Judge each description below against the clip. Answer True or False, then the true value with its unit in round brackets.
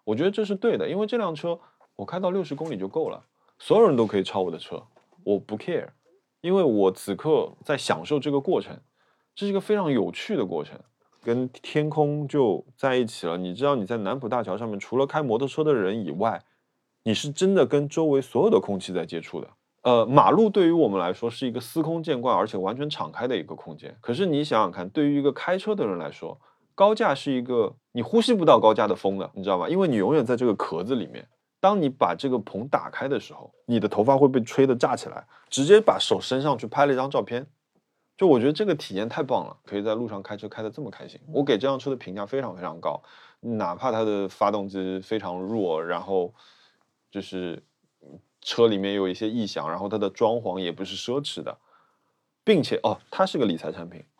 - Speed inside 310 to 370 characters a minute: True (330 characters per minute)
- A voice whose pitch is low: True (125 Hz)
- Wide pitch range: True (6.6 semitones)